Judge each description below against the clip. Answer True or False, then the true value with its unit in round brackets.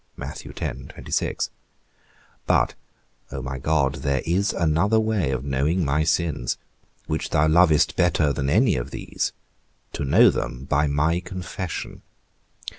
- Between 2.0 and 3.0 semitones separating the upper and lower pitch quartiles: False (4.3 semitones)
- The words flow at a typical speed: False (120 wpm)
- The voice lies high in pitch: False (75 Hz)